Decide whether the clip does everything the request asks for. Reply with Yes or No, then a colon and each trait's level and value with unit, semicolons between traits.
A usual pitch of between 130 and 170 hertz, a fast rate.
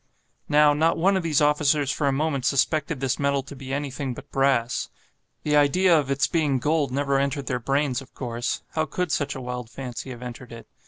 Yes: medium, 140 Hz; fast, 210 wpm